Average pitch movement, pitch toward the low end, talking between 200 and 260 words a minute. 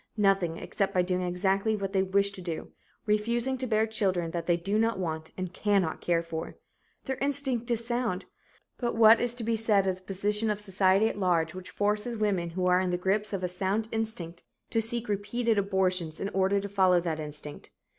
No: average, 3.4 semitones; high, 195 Hz; fast, 205 wpm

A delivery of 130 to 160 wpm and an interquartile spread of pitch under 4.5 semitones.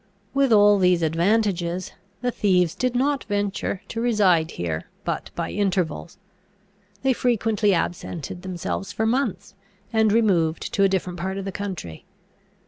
Yes: average, 140 wpm; average, 3.8 semitones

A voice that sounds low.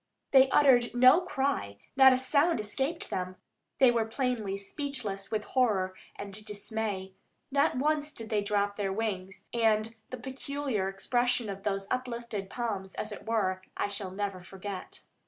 No: high, 220 Hz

